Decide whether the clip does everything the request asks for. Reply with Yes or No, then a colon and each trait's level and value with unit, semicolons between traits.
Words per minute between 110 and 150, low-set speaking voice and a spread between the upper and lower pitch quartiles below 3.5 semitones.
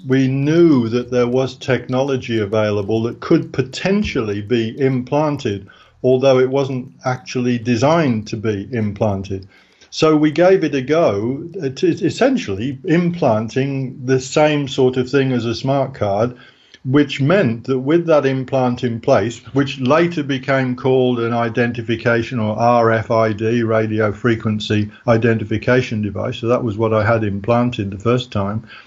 Yes: average, 140 wpm; low, 125 Hz; average, 3.1 semitones